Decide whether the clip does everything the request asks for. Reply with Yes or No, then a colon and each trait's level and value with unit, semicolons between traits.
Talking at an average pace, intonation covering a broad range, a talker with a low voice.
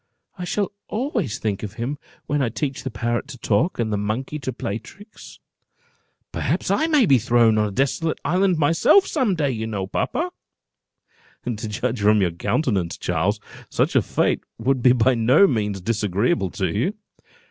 Yes: average, 175 wpm; wide, 6.7 semitones; low, 120 Hz